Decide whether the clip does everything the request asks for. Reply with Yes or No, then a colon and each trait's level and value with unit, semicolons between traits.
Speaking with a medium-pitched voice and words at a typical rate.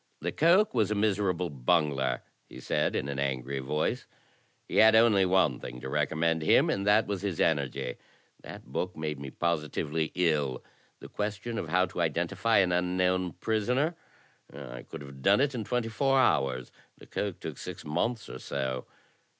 No: very low, 85 Hz; average, 170 wpm